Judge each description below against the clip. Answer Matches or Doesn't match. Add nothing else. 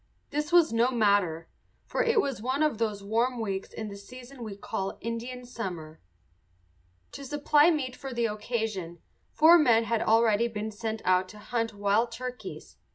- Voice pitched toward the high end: Matches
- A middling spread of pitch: Matches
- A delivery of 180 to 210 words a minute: Doesn't match